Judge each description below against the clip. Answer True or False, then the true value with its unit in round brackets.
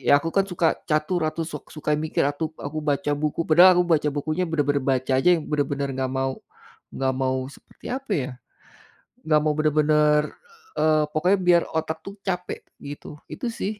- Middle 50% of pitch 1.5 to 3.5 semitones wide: True (2.5 semitones)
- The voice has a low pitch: False (155 Hz)